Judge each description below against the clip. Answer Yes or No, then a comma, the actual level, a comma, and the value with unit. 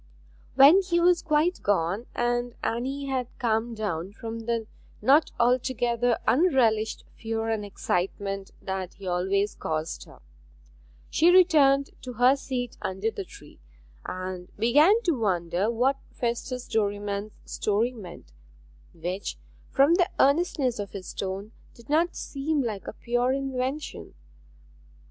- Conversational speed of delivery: No, slow, 130 wpm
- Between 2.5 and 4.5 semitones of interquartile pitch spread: No, average, 5.3 semitones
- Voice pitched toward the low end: No, high, 235 Hz